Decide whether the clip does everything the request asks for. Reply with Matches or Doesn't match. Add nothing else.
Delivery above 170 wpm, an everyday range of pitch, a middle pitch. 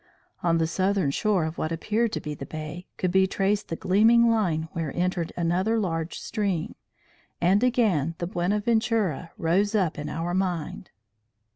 Doesn't match